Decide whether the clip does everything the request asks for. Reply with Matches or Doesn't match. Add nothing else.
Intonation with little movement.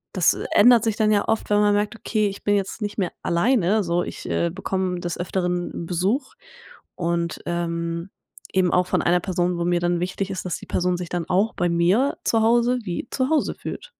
Doesn't match